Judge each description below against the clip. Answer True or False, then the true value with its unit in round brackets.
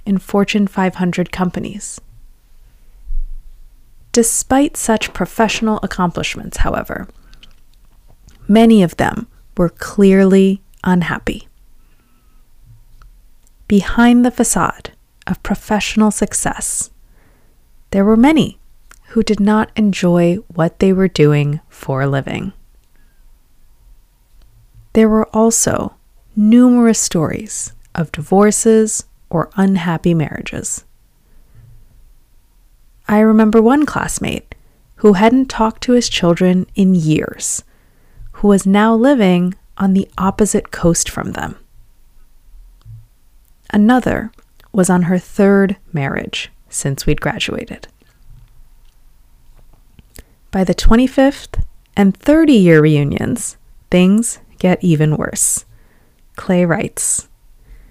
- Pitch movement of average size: False (7.8 semitones)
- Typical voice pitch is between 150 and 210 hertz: True (185 Hz)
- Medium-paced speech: False (90 wpm)